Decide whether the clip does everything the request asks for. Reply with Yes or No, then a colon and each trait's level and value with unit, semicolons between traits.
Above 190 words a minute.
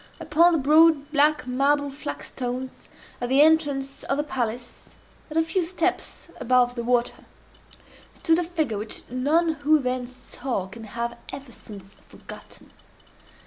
No: average, 145 wpm